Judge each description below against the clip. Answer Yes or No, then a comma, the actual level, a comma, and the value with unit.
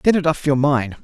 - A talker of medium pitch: Yes, medium, 145 Hz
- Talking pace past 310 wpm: No, fast, 290 wpm